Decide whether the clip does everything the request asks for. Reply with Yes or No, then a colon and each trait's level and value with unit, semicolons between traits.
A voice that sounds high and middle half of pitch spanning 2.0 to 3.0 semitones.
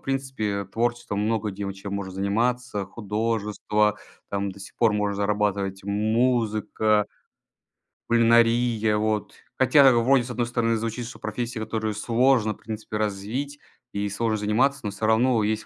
No: low, 110 Hz; narrow, 2.5 semitones